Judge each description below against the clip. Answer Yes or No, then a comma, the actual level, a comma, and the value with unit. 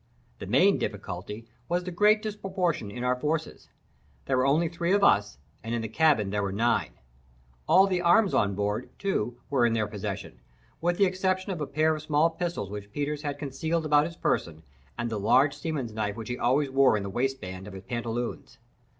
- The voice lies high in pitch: No, low, 135 Hz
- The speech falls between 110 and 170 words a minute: No, average, 200 wpm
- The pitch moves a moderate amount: No, wide, 7.9 semitones